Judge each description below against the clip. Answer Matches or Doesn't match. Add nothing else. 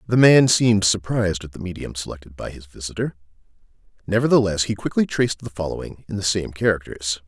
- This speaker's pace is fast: Doesn't match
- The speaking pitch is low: Matches